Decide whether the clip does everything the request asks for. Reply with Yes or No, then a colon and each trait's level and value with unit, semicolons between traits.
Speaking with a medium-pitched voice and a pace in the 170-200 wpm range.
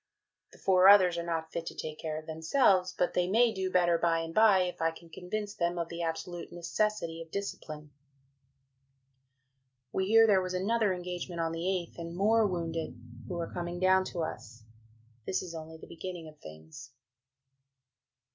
Yes: medium, 175 Hz; average, 180 wpm